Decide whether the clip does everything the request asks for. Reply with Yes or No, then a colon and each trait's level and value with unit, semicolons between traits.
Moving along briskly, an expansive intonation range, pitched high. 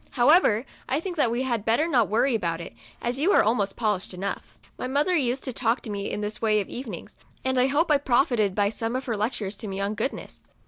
No: fast, 245 wpm; average, 4.1 semitones; high, 235 Hz